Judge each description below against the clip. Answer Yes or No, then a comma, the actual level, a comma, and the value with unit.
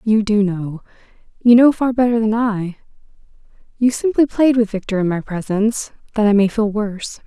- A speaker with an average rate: Yes, average, 175 wpm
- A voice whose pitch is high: Yes, high, 215 Hz